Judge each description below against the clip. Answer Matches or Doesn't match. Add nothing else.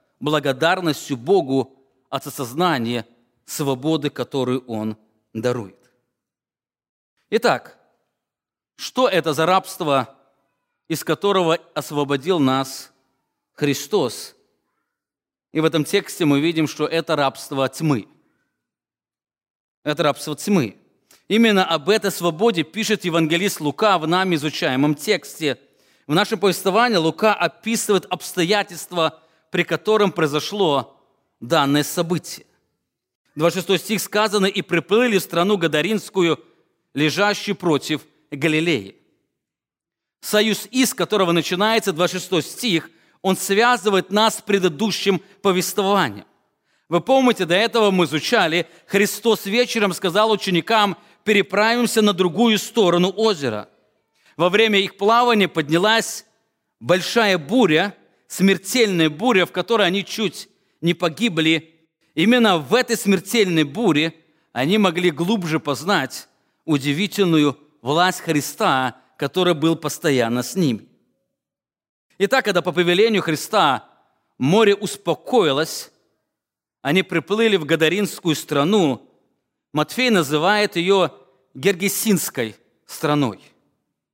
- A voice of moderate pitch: Matches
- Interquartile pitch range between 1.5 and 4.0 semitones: Doesn't match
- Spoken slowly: Matches